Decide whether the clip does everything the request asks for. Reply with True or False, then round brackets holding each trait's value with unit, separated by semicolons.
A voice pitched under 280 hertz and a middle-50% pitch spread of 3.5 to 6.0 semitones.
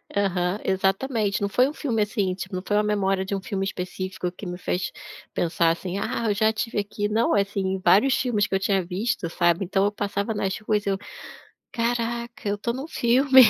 False (200 Hz; 2.8 semitones)